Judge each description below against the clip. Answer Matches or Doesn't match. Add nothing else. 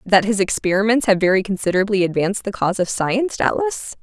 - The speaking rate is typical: Matches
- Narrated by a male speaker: Doesn't match